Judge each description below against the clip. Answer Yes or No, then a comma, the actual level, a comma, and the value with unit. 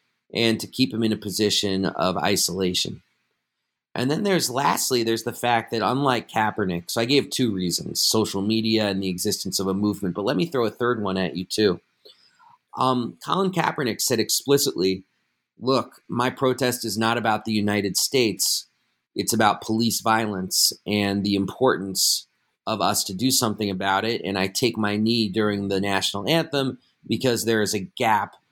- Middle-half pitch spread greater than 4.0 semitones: No, average, 3.6 semitones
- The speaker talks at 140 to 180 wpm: Yes, average, 175 wpm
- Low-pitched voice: Yes, low, 110 Hz